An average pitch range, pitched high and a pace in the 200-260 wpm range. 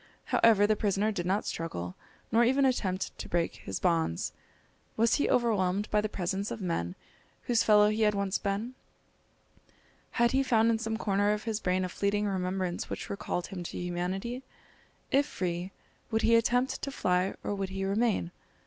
No: average, 3.5 semitones; high, 200 Hz; average, 175 wpm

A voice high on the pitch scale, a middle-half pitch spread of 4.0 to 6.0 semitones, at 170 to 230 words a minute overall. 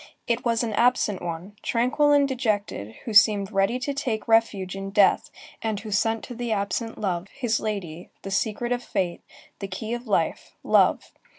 No: high, 215 Hz; average, 3.5 semitones; average, 180 wpm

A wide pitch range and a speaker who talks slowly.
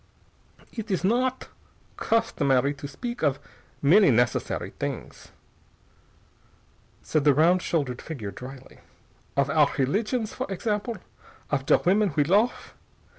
Yes: wide, 7.3 semitones; slow, 120 wpm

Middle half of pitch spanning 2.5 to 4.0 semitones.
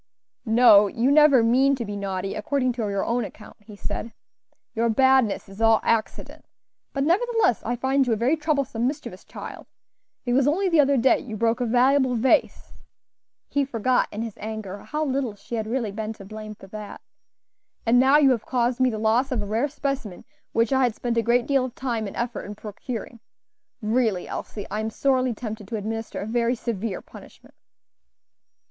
Yes: average, 3.4 semitones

